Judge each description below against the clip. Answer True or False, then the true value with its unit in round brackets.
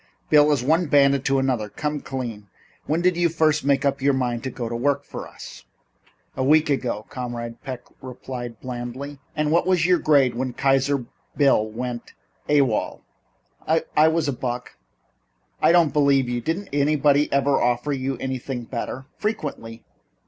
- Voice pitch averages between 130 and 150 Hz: True (135 Hz)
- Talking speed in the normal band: True (165 wpm)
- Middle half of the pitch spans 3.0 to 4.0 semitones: True (3.3 semitones)